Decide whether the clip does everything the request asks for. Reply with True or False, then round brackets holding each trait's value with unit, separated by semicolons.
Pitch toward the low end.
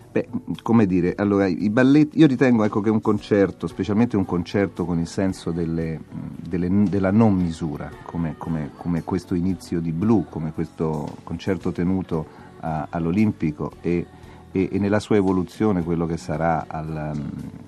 True (90 Hz)